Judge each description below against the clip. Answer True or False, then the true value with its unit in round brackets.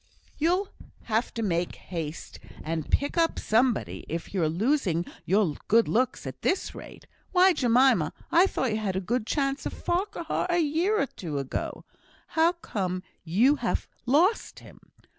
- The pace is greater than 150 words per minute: True (160 wpm)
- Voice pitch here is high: True (240 Hz)